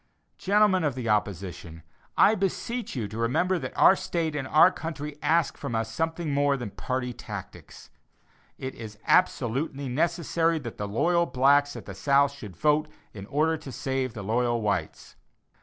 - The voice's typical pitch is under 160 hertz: Yes, medium, 140 Hz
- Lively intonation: Yes, wide, 5.9 semitones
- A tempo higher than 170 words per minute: No, average, 165 wpm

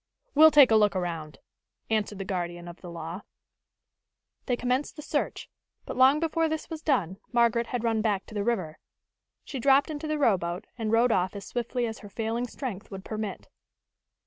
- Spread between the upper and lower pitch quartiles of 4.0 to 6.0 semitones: Yes, average, 5.2 semitones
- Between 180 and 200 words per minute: Yes, average, 185 wpm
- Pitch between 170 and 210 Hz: No, high, 225 Hz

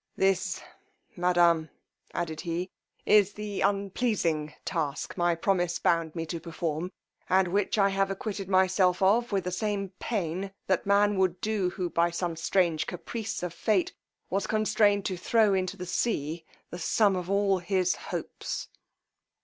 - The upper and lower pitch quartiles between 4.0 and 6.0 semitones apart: No, narrow, 2.6 semitones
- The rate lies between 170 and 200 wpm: No, average, 150 wpm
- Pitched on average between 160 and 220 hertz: Yes, medium, 185 Hz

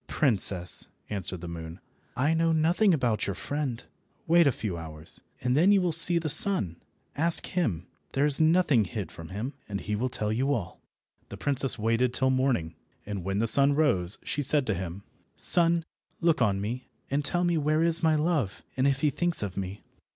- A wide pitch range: Yes, wide, 7.9 semitones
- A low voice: Yes, low, 130 Hz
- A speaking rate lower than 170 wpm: No, average, 195 wpm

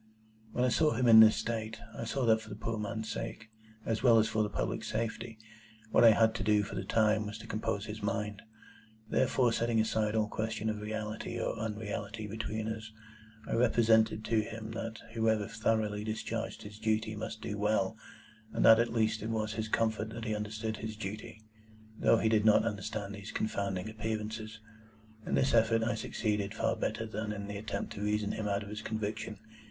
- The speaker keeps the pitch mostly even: Yes, narrow, 1.0 semitones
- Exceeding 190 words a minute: Yes, average, 200 wpm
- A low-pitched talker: Yes, low, 110 Hz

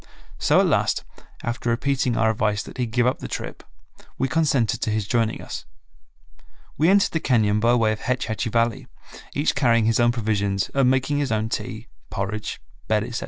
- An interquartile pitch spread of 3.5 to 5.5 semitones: No, average, 2.8 semitones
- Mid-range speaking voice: No, low, 115 Hz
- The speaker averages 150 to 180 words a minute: No, average, 190 wpm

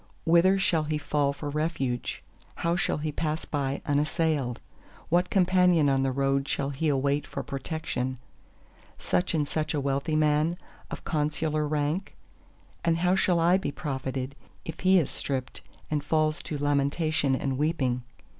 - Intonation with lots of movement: No, average, 2.8 semitones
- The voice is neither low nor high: Yes, medium, 150 Hz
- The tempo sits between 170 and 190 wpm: No, average, 150 wpm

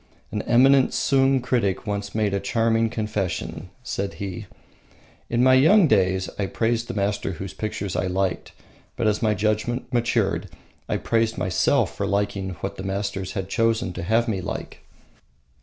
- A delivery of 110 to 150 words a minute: No, average, 160 wpm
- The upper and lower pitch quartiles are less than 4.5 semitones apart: Yes, average, 3.3 semitones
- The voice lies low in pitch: Yes, low, 105 Hz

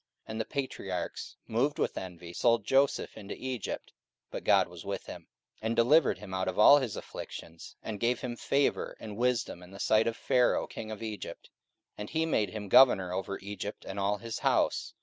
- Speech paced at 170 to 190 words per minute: No, average, 200 wpm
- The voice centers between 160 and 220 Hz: No, low, 110 Hz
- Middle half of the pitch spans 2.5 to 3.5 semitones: No, average, 4.0 semitones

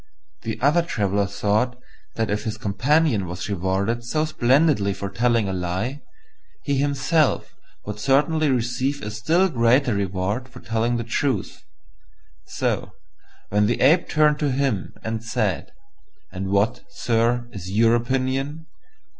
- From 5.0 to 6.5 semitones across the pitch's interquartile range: Yes, average, 5.3 semitones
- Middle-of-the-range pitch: No, low, 120 Hz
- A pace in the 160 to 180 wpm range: No, average, 140 wpm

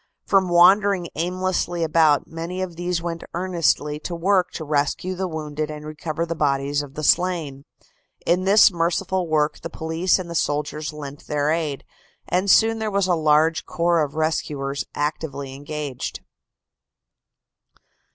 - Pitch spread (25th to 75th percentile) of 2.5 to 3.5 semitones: Yes, average, 3.1 semitones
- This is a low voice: No, medium, 165 Hz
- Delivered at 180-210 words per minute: No, average, 150 wpm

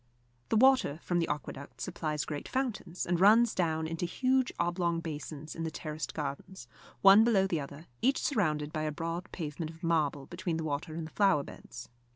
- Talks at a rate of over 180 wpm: Yes, average, 190 wpm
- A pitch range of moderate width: Yes, average, 3.8 semitones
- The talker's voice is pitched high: No, medium, 165 Hz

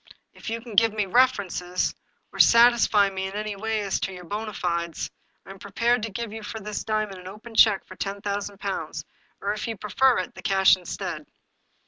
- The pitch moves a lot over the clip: No, narrow, 2.5 semitones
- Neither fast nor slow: No, fast, 210 wpm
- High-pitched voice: Yes, high, 205 Hz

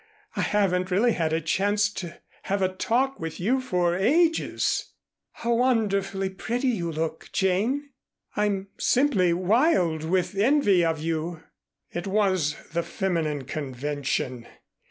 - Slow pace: Yes, slow, 130 wpm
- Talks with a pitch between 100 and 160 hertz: No, high, 190 Hz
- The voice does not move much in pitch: No, average, 4.7 semitones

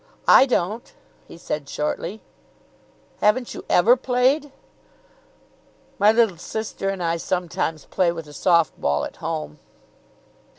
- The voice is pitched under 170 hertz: No, medium, 185 Hz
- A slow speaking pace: Yes, slow, 125 wpm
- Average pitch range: No, wide, 5.7 semitones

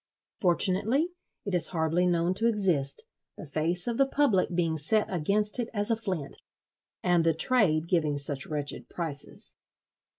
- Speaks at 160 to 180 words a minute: No, average, 145 wpm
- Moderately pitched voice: Yes, medium, 180 Hz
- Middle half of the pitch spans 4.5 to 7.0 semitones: Yes, average, 4.8 semitones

